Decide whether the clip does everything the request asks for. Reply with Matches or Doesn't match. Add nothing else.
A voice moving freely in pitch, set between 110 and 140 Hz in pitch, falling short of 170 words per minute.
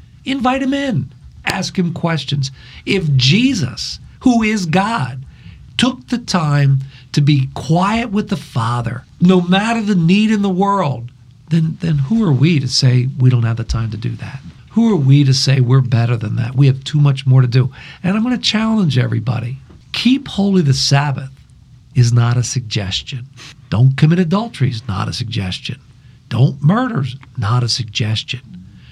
Doesn't match